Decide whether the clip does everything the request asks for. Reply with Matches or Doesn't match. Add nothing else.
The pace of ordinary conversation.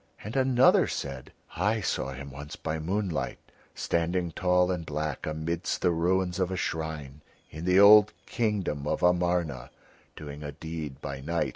Matches